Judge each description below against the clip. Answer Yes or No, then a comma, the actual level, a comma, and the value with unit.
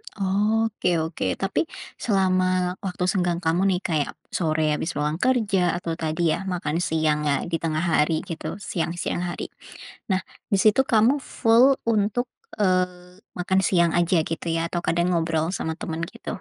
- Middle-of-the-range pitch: Yes, medium, 180 Hz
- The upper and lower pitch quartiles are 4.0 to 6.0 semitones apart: No, average, 2.9 semitones